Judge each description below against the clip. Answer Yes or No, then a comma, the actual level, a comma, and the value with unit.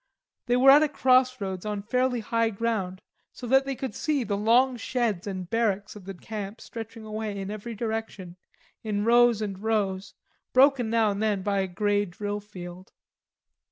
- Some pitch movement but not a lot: Yes, average, 3.3 semitones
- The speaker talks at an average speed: Yes, average, 180 wpm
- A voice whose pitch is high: Yes, high, 215 Hz